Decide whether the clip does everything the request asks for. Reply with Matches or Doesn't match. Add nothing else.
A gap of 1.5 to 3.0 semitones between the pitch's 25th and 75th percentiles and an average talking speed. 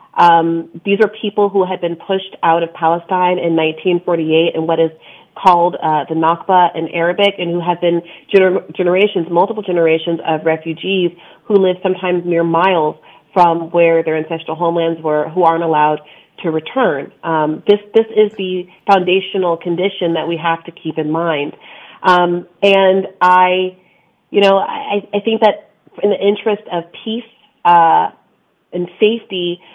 Matches